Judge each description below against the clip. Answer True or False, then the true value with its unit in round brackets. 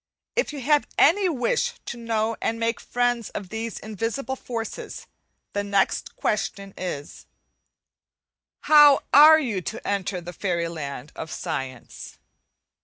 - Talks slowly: True (130 wpm)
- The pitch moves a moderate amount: False (6.2 semitones)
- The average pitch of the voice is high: True (225 Hz)